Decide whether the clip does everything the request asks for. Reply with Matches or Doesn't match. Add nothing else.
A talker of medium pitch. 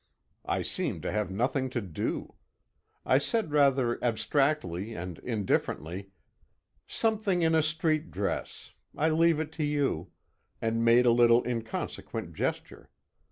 Doesn't match